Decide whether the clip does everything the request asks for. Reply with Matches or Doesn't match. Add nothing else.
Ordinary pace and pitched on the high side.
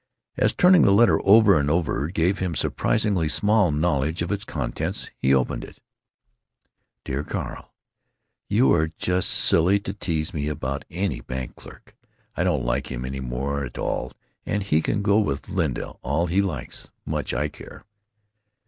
Doesn't match